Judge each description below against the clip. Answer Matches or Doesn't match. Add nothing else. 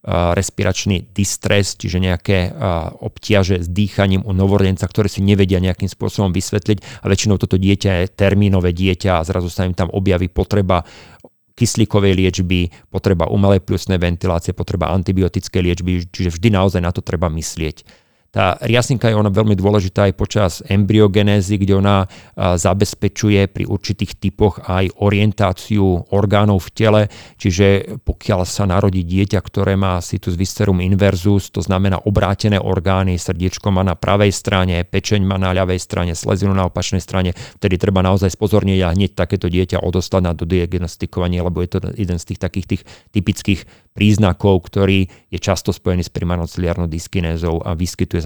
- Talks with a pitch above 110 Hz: Doesn't match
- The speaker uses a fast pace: Doesn't match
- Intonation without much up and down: Matches